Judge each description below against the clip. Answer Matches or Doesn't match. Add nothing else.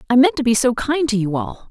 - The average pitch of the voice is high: Matches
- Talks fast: Matches